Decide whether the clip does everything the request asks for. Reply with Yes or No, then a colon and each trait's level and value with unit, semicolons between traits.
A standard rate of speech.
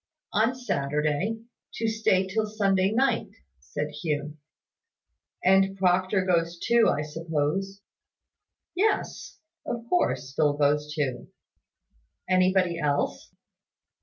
No: slow, 100 wpm